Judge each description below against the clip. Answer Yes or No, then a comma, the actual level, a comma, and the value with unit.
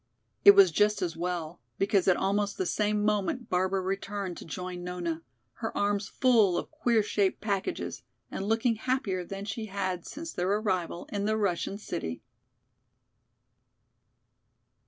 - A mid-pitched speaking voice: No, high, 200 Hz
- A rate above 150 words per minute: No, average, 145 wpm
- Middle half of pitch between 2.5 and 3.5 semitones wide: Yes, average, 2.8 semitones